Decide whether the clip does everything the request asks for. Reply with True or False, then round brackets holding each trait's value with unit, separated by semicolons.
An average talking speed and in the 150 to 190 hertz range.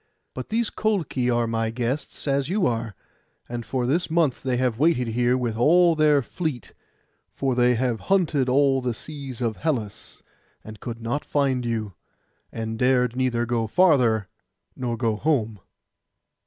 False (155 wpm; 125 Hz)